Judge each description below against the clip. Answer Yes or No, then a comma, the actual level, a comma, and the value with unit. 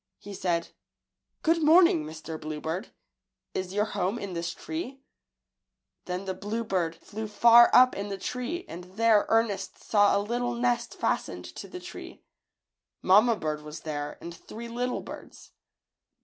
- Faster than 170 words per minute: No, average, 150 wpm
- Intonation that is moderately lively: No, wide, 5.8 semitones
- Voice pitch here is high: Yes, high, 205 Hz